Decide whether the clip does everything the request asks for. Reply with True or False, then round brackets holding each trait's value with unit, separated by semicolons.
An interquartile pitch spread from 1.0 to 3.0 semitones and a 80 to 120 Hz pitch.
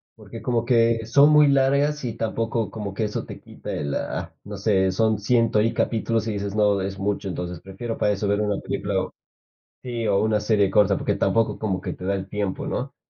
True (2.6 semitones; 105 Hz)